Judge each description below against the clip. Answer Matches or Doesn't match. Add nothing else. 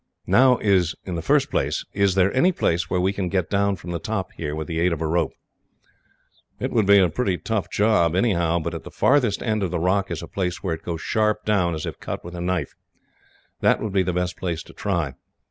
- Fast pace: Matches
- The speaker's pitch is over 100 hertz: Doesn't match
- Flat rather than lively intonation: Doesn't match